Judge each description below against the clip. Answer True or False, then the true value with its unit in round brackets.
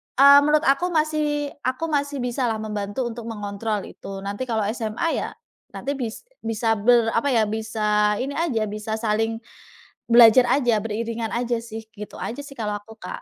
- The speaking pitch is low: False (230 Hz)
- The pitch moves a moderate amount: True (3.7 semitones)